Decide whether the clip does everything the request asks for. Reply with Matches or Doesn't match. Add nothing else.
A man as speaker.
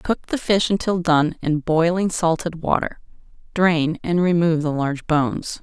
Doesn't match